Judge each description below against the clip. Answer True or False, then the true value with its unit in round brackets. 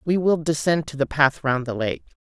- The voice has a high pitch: False (145 Hz)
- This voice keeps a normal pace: False (240 wpm)